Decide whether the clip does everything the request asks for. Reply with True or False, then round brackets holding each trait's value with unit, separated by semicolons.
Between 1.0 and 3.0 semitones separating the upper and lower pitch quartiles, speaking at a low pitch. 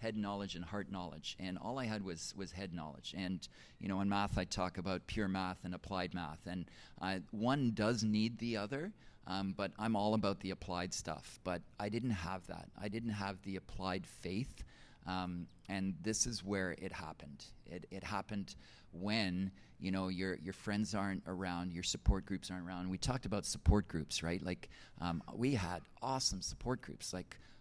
True (2.4 semitones; 95 Hz)